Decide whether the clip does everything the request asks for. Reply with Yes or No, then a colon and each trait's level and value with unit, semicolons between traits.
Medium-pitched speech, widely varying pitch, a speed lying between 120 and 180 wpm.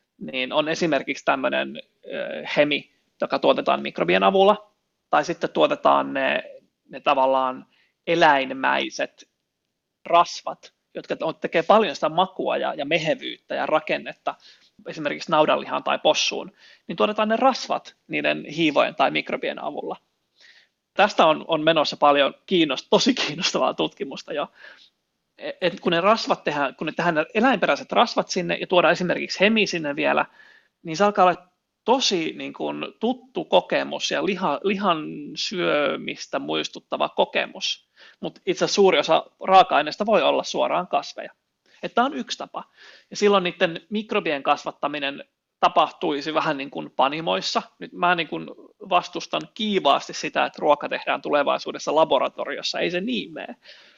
Yes: medium, 180 Hz; wide, 5.8 semitones; average, 135 wpm